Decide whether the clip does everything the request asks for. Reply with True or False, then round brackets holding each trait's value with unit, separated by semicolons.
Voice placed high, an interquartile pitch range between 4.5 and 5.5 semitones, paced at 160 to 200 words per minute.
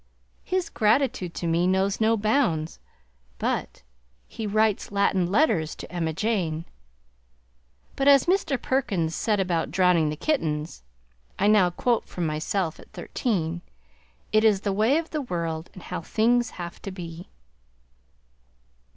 False (195 Hz; 5.1 semitones; 140 wpm)